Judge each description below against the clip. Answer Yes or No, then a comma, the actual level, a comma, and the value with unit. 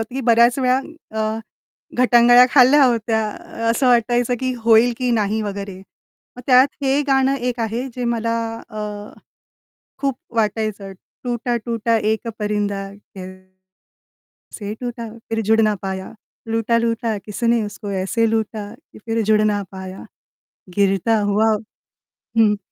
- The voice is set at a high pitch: Yes, high, 225 Hz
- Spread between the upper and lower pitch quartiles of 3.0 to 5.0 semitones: No, narrow, 2.6 semitones